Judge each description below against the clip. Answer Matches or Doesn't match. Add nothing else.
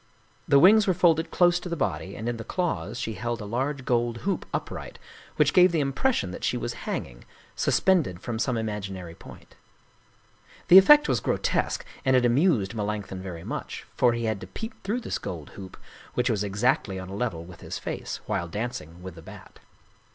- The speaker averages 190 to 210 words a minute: Matches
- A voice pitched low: Matches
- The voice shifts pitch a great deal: Matches